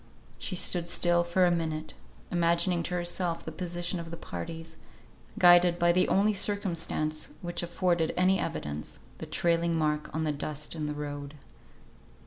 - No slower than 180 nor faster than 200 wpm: No, average, 155 wpm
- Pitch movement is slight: Yes, narrow, 2.1 semitones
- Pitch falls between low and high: Yes, medium, 170 Hz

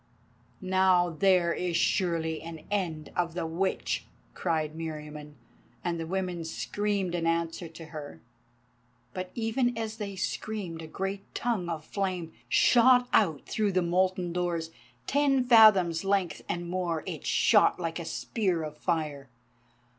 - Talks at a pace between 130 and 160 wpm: Yes, average, 140 wpm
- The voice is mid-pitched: Yes, medium, 175 Hz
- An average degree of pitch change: Yes, average, 3.3 semitones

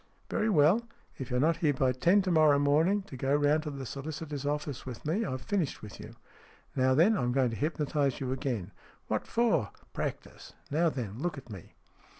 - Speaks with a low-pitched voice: No, medium, 145 Hz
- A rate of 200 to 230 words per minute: Yes, fast, 205 wpm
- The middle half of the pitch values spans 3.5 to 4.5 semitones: Yes, average, 3.9 semitones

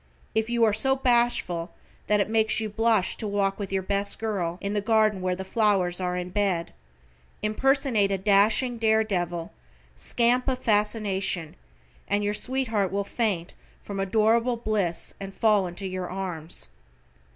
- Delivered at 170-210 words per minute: No, average, 160 wpm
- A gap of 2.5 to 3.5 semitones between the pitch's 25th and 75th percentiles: Yes, average, 2.8 semitones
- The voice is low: No, high, 205 Hz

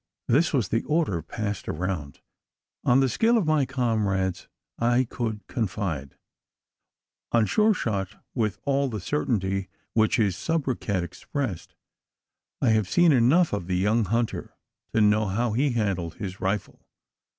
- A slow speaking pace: No, average, 145 wpm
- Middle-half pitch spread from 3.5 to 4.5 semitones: No, average, 5.2 semitones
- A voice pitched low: Yes, low, 110 Hz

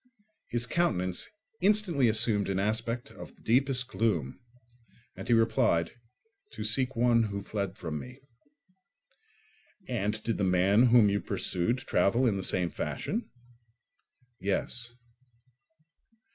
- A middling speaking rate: No, slow, 120 wpm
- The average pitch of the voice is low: Yes, low, 115 Hz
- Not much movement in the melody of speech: No, average, 4.0 semitones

